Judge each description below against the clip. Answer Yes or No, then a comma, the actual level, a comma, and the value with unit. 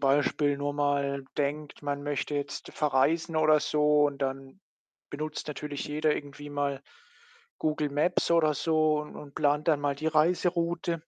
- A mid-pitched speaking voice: Yes, medium, 150 Hz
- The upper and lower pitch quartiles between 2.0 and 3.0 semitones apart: No, narrow, 1.4 semitones